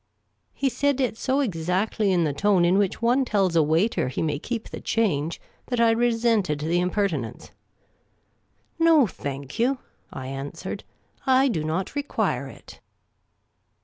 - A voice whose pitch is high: Yes, high, 200 Hz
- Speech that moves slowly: No, average, 165 wpm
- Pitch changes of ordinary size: No, wide, 7.1 semitones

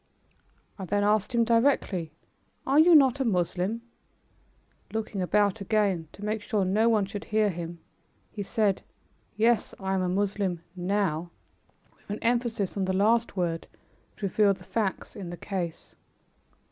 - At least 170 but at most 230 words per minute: No, average, 155 wpm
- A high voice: Yes, high, 205 Hz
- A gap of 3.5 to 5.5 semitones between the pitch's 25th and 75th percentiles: No, average, 3.0 semitones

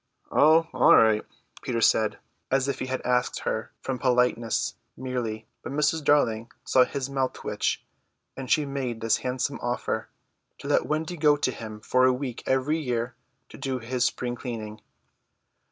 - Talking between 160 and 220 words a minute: Yes, average, 165 wpm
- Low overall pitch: Yes, low, 125 Hz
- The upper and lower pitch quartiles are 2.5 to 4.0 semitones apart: Yes, average, 2.8 semitones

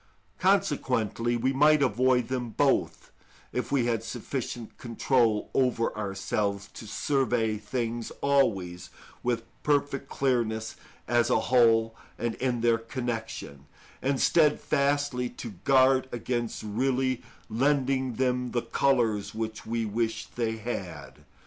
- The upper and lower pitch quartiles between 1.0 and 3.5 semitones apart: Yes, average, 2.7 semitones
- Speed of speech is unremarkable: No, slow, 115 wpm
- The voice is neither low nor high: No, low, 120 Hz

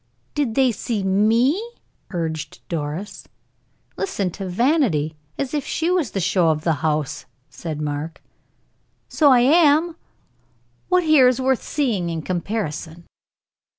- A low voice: No, high, 205 Hz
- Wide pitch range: Yes, wide, 8.9 semitones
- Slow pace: Yes, slow, 130 wpm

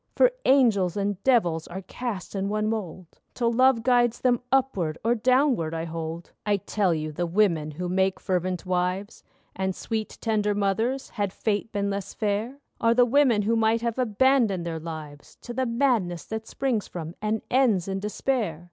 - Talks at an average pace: Yes, average, 175 wpm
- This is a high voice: Yes, high, 205 Hz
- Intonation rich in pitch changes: No, average, 4.7 semitones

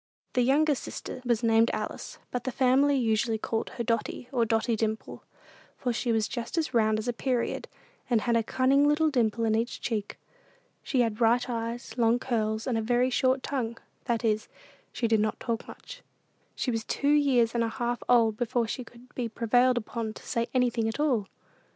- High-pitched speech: Yes, high, 235 Hz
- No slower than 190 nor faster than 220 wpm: Yes, average, 195 wpm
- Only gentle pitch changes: Yes, narrow, 2.2 semitones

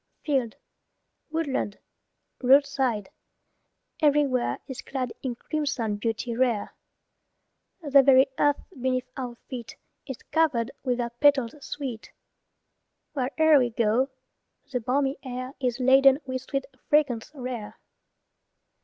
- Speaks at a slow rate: Yes, slow, 110 wpm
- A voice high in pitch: Yes, very high, 260 Hz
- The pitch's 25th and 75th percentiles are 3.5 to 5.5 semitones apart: No, narrow, 2.5 semitones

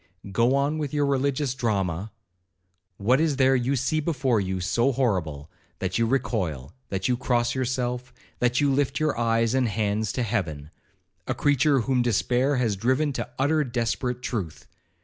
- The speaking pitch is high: No, low, 125 Hz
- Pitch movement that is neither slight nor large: Yes, average, 4.6 semitones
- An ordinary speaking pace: Yes, average, 160 wpm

